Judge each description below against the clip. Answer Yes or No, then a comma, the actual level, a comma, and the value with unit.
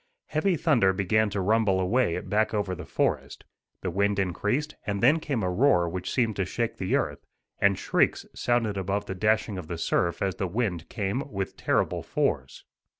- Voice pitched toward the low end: Yes, low, 100 Hz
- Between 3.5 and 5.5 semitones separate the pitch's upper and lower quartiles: Yes, average, 3.8 semitones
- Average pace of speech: Yes, average, 185 wpm